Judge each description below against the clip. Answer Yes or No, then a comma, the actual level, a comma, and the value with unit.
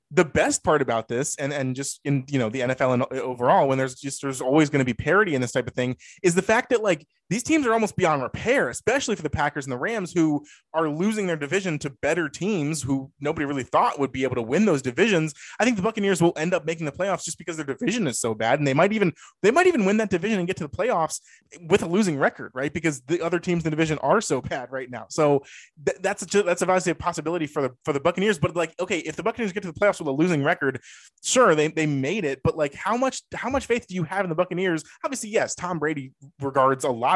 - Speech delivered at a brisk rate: Yes, fast, 270 wpm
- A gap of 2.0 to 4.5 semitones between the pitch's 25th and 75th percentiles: No, average, 5.1 semitones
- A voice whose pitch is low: No, medium, 160 Hz